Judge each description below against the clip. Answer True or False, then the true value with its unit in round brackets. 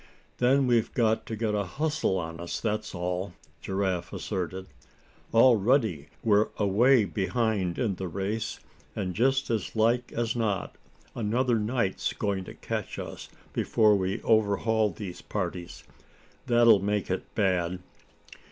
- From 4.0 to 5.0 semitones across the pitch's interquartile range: False (3.6 semitones)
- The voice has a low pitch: True (105 Hz)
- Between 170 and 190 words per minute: False (135 wpm)